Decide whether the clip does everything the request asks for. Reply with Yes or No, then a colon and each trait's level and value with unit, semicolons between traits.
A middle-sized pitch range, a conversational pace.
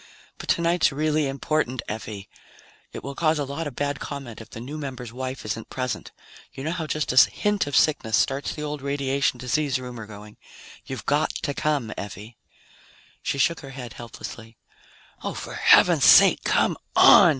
Yes: average, 3.9 semitones; average, 175 wpm